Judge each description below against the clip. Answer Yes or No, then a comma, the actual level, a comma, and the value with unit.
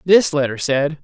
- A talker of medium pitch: Yes, medium, 150 Hz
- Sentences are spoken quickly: No, average, 175 wpm